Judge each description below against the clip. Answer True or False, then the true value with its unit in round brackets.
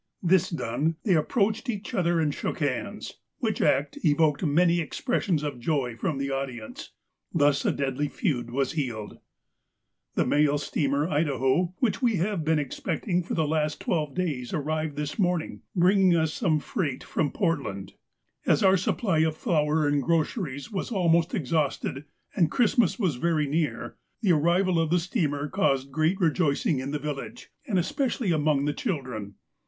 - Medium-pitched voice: True (155 Hz)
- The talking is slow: False (160 wpm)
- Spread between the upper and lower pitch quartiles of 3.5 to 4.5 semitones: True (4.0 semitones)